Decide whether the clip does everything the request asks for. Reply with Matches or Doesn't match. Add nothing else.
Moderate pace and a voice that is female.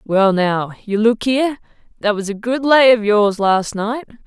Matches